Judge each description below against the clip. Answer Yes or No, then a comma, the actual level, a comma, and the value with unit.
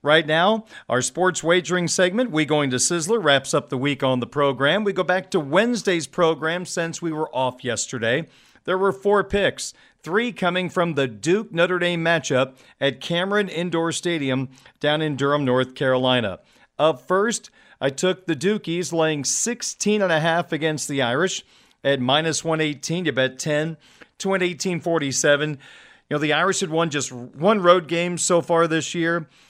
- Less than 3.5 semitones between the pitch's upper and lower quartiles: No, average, 4.3 semitones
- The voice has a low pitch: No, medium, 165 Hz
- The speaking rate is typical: Yes, average, 165 wpm